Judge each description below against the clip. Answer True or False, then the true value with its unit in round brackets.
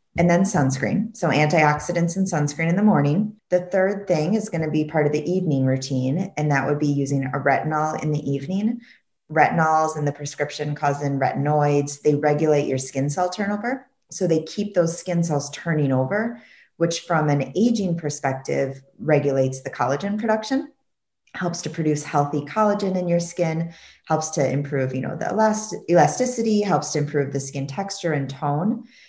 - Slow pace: False (175 wpm)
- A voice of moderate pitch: True (155 Hz)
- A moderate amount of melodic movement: True (4.7 semitones)